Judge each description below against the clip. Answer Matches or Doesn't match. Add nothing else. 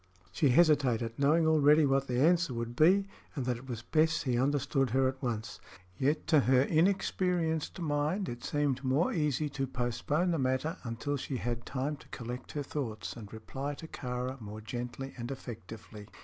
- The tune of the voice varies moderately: Matches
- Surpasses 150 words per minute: Matches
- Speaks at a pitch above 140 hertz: Doesn't match